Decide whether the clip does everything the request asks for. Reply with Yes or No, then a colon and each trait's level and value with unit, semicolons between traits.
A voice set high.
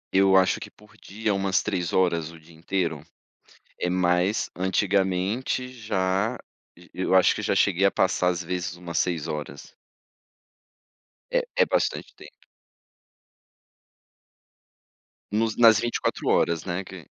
No: very low, 95 Hz